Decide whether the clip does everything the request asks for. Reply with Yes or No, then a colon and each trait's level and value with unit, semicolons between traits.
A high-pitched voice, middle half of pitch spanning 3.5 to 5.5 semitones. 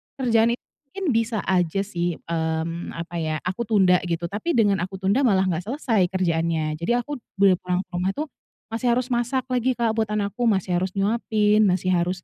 Yes: high, 195 Hz; average, 4.5 semitones